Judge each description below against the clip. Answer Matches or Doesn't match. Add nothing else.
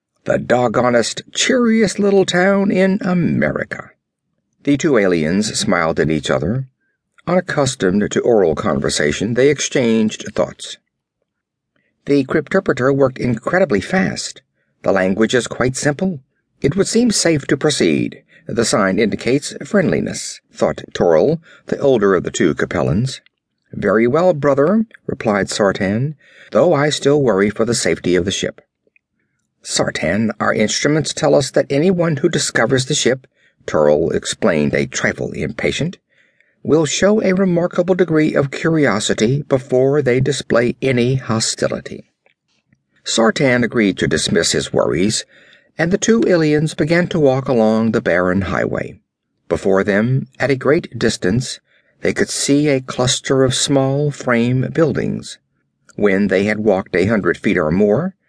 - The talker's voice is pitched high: Doesn't match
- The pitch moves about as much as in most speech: Doesn't match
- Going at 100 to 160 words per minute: Matches